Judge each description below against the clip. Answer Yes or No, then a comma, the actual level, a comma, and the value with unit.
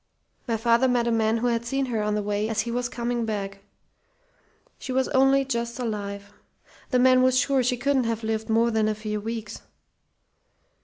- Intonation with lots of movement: No, narrow, 2.5 semitones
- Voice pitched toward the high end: Yes, high, 235 Hz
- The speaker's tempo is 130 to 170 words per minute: No, average, 195 wpm